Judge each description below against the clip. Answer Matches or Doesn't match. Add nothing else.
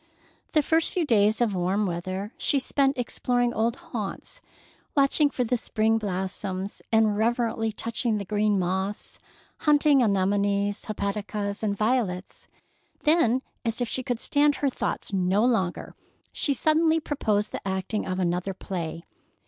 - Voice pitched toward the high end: Matches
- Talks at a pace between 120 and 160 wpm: Matches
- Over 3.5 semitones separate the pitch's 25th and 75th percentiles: Matches